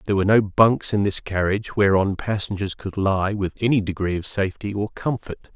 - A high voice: No, low, 100 Hz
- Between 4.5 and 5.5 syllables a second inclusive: No, 5.7 syllables/s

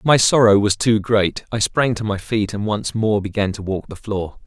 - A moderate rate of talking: No, fast, 240 wpm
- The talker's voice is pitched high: No, low, 105 Hz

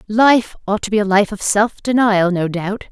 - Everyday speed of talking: No, fast, 225 wpm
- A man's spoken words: No, female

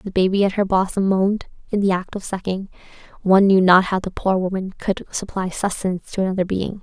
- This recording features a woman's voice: Yes, female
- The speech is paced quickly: Yes, fast, 210 wpm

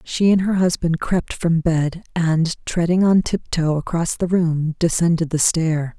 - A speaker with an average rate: Yes, average, 170 wpm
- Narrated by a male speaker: No, female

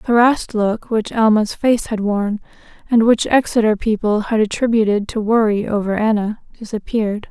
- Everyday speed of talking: Yes, average, 155 wpm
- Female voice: Yes, female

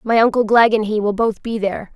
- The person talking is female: Yes, female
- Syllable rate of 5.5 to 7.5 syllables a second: Yes, 6.0 syllables/s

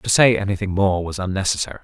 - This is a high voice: No, very low, 95 Hz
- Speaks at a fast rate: No, average, 195 wpm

